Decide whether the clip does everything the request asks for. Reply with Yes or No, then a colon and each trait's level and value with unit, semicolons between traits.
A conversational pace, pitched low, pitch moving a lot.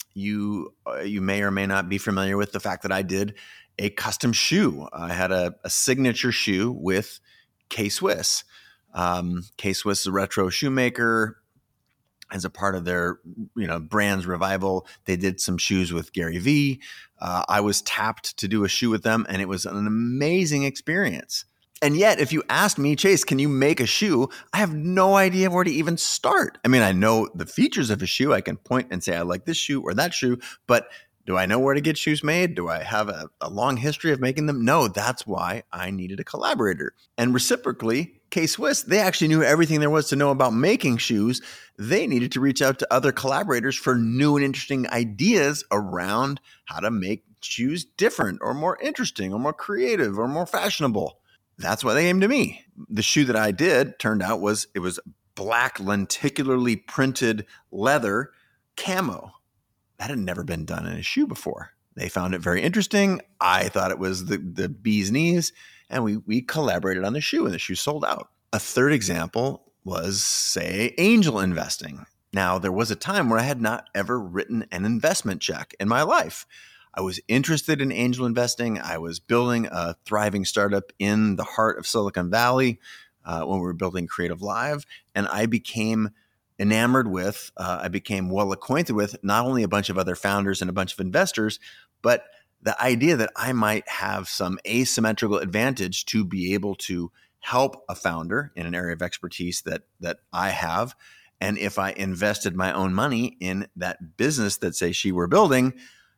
Yes: average, 195 wpm; low, 110 Hz; wide, 5.7 semitones